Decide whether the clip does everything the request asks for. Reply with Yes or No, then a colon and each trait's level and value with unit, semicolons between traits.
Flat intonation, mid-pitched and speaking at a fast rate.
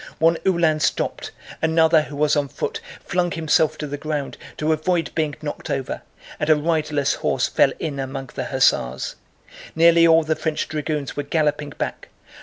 No: narrow, 1.8 semitones; medium, 155 Hz; average, 170 wpm